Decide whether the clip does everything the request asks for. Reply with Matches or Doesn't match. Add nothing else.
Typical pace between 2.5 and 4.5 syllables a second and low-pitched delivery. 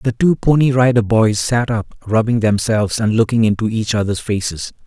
Doesn't match